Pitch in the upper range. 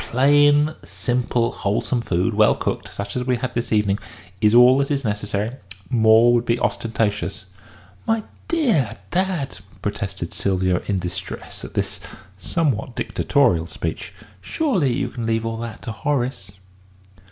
No: low, 115 Hz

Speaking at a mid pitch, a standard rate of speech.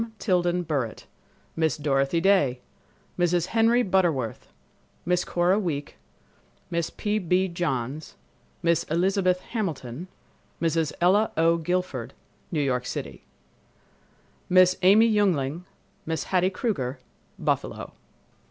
No: medium, 175 Hz; slow, 105 wpm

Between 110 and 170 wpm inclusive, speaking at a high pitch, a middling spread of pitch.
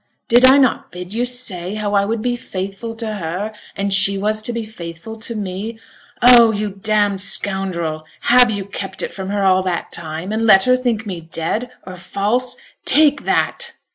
No: average, 190 wpm; high, 205 Hz; average, 3.3 semitones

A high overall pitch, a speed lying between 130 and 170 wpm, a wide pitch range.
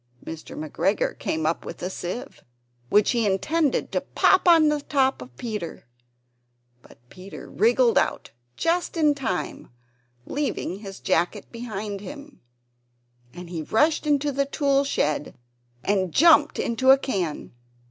Yes: high, 235 Hz; slow, 135 wpm; wide, 7.4 semitones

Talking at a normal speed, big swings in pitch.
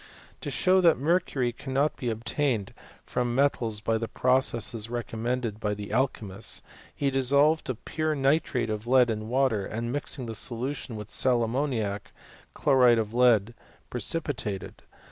No: average, 150 wpm; average, 3.4 semitones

